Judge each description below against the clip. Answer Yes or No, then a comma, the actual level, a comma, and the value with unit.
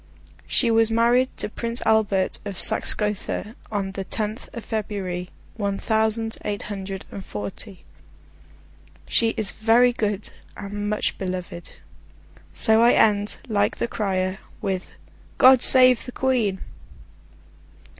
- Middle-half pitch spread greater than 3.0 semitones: No, narrow, 2.6 semitones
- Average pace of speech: No, slow, 125 wpm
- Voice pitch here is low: No, high, 210 Hz